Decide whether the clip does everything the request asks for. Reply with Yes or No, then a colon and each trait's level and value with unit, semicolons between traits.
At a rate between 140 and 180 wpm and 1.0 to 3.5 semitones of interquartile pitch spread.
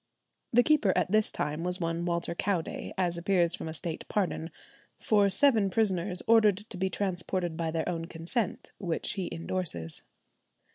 Yes: average, 160 wpm; average, 3.2 semitones